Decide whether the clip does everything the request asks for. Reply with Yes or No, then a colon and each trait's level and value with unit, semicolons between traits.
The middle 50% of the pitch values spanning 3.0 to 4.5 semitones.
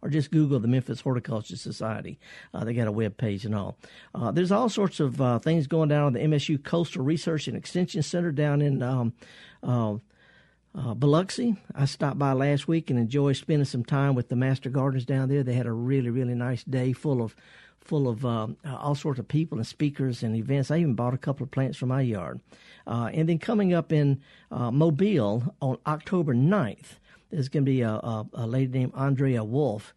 Yes: average, 4.0 semitones